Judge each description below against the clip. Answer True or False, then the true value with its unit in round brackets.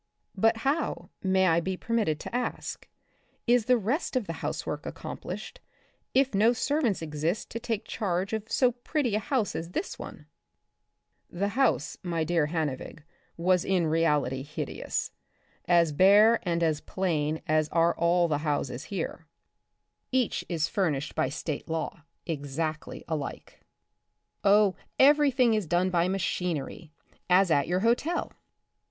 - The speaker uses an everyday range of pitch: False (5.9 semitones)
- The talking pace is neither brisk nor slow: True (150 wpm)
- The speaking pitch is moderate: True (180 Hz)